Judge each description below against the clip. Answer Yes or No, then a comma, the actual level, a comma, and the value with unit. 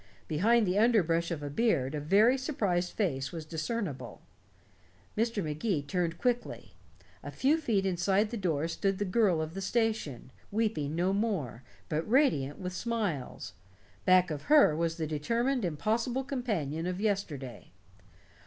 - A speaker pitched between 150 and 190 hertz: Yes, medium, 185 Hz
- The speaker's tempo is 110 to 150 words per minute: Yes, average, 145 wpm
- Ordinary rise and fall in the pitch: No, wide, 6.4 semitones